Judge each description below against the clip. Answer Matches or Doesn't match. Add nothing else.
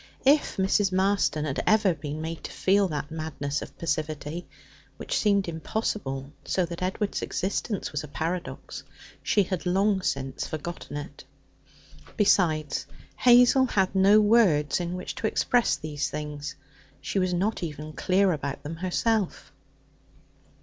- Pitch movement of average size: Matches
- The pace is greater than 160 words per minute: Doesn't match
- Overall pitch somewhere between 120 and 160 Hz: Doesn't match